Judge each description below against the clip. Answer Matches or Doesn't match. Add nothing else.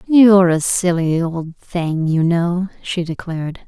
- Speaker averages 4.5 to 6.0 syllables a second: Doesn't match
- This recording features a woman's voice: Matches